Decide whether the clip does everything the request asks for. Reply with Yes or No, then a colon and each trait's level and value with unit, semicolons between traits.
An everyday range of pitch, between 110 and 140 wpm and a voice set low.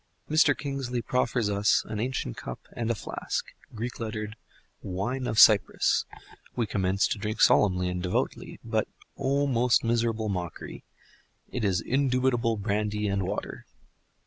Yes: average, 3.4 semitones; slow, 135 wpm; low, 110 Hz